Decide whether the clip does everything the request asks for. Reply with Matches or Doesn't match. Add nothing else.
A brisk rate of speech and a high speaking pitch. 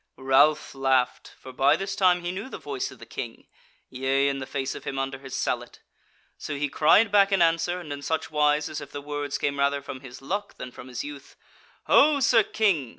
Doesn't match